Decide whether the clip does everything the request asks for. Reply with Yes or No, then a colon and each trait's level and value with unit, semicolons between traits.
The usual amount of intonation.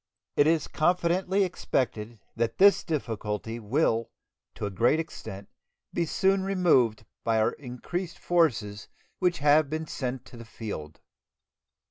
No: wide, 7.2 semitones